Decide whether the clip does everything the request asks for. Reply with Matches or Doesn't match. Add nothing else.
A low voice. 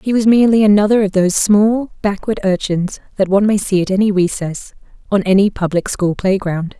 Doesn't match